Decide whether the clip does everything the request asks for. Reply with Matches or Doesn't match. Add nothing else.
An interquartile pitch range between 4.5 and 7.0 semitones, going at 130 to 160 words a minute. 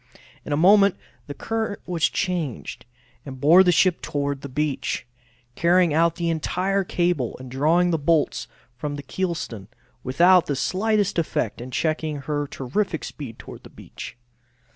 Doesn't match